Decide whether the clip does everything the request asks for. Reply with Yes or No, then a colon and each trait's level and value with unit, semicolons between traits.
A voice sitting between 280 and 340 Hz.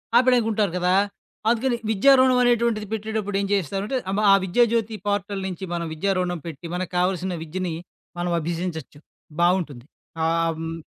No: high, 190 Hz